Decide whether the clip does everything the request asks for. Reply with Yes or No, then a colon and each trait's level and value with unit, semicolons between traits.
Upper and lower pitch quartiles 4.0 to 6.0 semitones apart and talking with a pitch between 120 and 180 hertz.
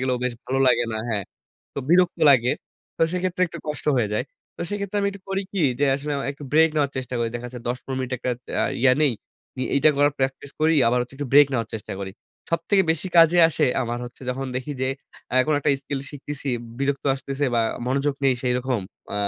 No: average, 3.4 semitones; low, 135 Hz